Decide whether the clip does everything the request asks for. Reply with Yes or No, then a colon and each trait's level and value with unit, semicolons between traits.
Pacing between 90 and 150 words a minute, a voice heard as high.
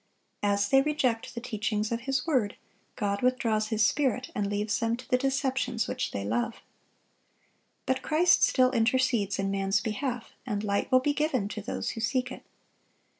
No: average, 175 wpm; high, 235 Hz